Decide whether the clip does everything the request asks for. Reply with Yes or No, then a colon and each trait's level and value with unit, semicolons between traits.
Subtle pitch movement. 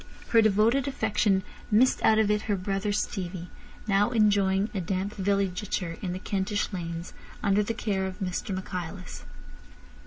Yes: narrow, 2.1 semitones